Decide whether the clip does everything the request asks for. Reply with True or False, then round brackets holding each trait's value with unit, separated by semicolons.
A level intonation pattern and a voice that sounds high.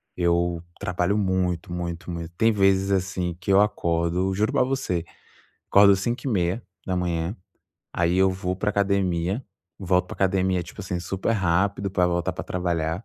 False (2.2 semitones; 90 Hz)